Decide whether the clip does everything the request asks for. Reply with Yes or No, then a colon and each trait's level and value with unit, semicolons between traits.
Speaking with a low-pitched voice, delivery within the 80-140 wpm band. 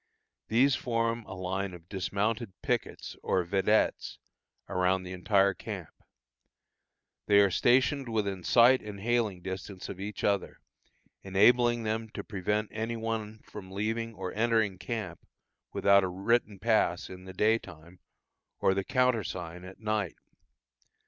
Yes: low, 100 Hz; slow, 135 wpm